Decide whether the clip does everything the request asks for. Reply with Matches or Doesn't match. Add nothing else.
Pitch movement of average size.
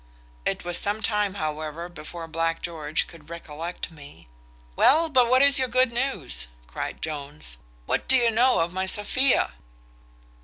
Doesn't match